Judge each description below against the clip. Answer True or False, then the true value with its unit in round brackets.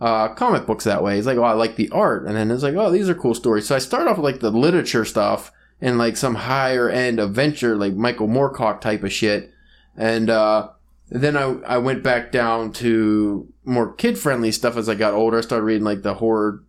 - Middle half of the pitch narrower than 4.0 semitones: True (2.8 semitones)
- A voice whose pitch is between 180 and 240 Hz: False (115 Hz)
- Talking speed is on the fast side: True (235 wpm)